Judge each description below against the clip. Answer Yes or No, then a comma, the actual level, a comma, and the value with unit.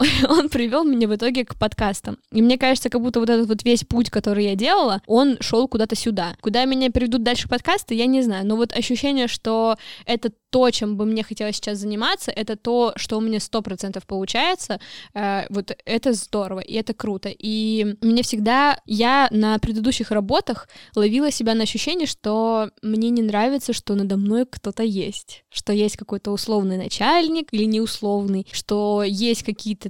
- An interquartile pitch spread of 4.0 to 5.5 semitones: No, average, 2.7 semitones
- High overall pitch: Yes, high, 225 Hz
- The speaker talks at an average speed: No, fast, 175 wpm